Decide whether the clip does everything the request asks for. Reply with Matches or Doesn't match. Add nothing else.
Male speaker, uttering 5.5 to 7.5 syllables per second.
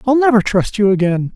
Matches